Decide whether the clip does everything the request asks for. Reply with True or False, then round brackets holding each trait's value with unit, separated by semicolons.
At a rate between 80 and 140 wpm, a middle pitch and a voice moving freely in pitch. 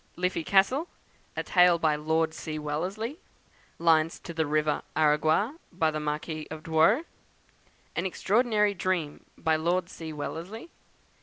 False (135 wpm; 165 Hz; 3.5 semitones)